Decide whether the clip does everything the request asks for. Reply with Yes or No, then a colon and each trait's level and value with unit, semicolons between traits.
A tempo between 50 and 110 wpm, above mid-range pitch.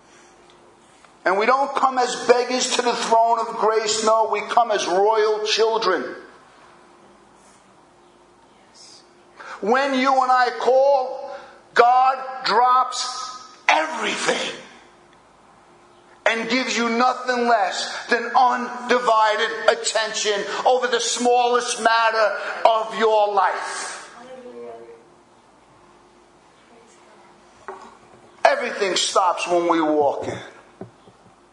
Yes: slow, 90 wpm; high, 235 Hz